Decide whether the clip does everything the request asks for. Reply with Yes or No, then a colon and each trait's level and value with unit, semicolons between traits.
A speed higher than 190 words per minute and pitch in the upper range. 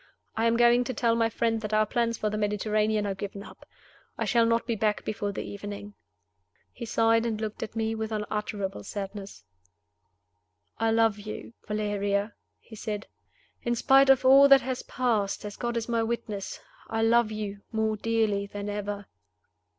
No: average, 175 wpm; high, 220 Hz